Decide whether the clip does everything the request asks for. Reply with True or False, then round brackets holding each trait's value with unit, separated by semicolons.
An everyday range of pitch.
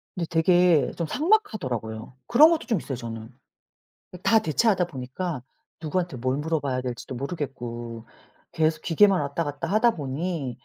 False (6.0 semitones)